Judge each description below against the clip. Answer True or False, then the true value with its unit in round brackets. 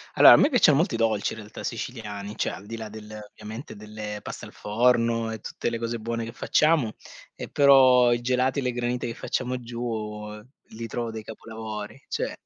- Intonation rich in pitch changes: False (2.4 semitones)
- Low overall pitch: True (115 Hz)